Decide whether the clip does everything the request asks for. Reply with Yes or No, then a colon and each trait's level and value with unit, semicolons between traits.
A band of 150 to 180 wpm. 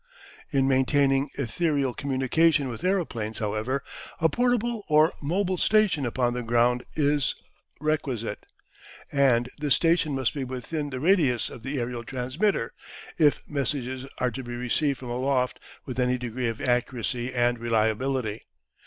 No: average, 140 wpm